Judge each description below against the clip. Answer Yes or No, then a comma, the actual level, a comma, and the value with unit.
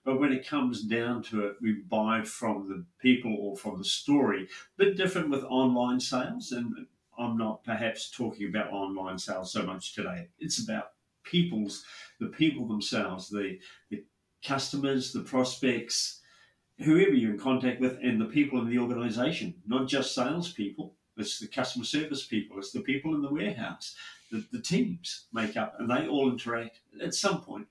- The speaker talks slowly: No, average, 175 wpm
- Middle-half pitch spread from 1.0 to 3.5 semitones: No, average, 4.8 semitones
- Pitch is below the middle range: Yes, low, 125 Hz